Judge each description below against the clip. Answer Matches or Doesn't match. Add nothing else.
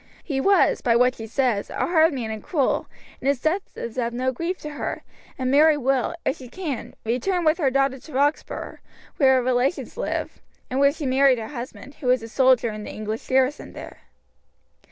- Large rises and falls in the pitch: Doesn't match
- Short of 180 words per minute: Doesn't match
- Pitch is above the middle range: Matches